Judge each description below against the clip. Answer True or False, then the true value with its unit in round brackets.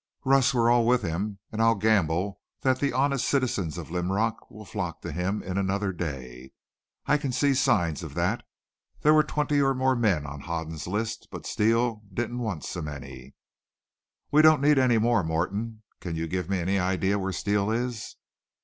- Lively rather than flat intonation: True (5.8 semitones)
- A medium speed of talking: True (185 wpm)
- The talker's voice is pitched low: True (105 Hz)